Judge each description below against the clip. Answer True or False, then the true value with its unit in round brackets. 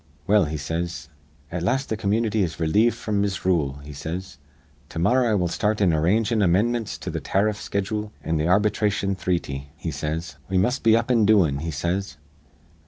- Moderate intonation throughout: True (4.7 semitones)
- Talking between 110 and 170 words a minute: False (185 wpm)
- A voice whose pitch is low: True (95 Hz)